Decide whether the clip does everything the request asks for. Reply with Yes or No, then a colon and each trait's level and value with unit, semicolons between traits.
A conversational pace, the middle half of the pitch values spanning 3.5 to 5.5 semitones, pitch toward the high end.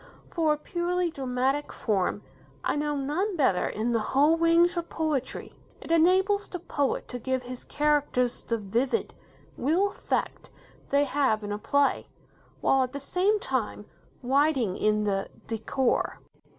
Yes: average, 150 wpm; average, 5.1 semitones; very high, 280 Hz